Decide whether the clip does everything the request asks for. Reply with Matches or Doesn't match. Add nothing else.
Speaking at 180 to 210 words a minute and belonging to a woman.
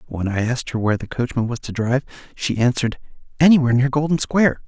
Doesn't match